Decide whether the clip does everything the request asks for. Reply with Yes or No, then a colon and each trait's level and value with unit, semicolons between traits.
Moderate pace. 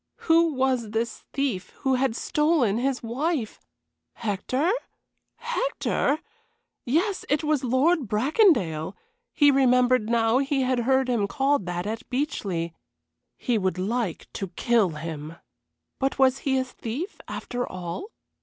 No: slow, 130 wpm